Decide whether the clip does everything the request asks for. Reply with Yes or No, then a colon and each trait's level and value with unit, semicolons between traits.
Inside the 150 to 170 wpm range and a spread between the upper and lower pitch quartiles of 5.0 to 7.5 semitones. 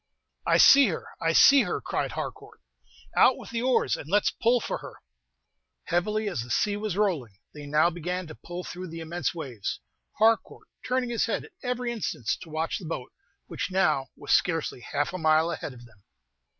No: average, 190 wpm; wide, 5.6 semitones